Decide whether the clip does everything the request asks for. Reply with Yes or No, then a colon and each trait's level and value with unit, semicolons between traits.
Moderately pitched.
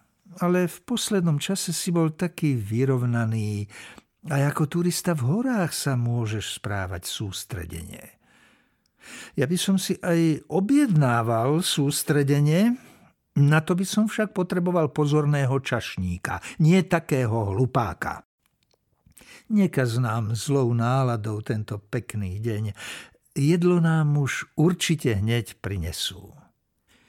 Yes: medium, 145 Hz